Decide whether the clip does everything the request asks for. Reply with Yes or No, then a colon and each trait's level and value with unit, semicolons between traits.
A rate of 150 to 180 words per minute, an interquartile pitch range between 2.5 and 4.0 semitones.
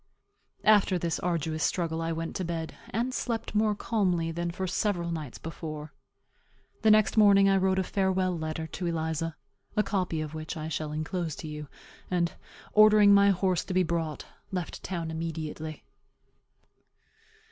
Yes: average, 160 wpm; average, 3.3 semitones